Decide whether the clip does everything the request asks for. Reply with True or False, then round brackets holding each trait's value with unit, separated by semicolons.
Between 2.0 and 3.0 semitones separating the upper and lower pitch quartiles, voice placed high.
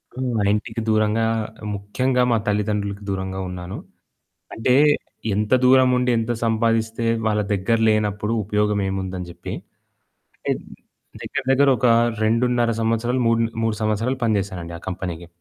False (2.7 semitones; 110 Hz)